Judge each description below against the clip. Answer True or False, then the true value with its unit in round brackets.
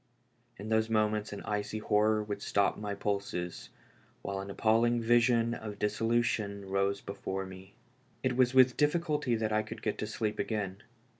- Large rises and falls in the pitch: False (2.4 semitones)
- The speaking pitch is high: False (105 Hz)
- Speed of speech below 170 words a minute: True (160 wpm)